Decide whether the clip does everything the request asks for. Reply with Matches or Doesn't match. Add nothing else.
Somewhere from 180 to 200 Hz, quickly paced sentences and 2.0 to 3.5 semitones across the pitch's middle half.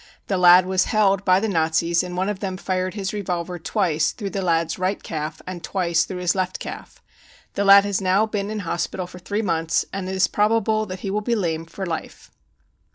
Matches